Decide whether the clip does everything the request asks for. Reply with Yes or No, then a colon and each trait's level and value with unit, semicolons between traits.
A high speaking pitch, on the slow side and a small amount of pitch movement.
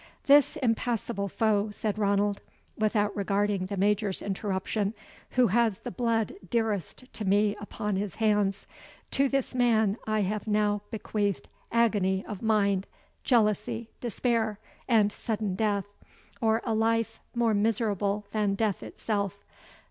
Yes: high, 210 Hz; slow, 130 wpm; narrow, 1.9 semitones